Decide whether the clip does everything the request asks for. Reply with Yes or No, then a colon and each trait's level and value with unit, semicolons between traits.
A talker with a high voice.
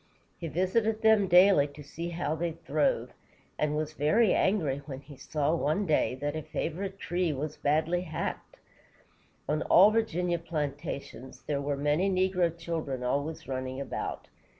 No: medium, 160 Hz